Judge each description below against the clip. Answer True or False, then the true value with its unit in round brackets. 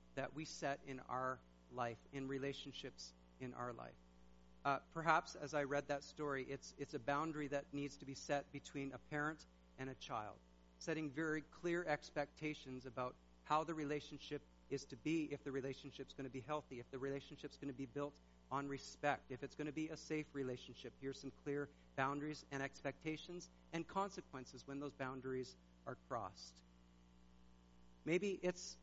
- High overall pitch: False (140 Hz)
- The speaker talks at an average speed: True (175 wpm)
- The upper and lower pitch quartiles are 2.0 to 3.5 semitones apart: True (3.2 semitones)